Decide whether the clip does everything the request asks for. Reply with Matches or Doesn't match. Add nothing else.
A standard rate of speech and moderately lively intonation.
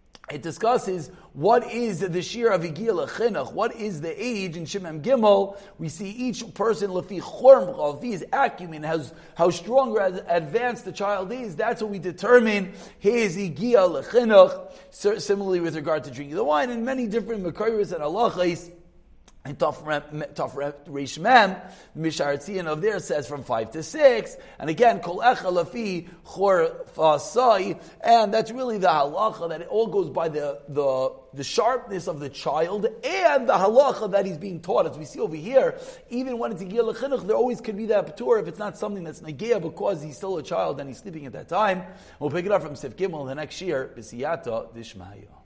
Doesn't match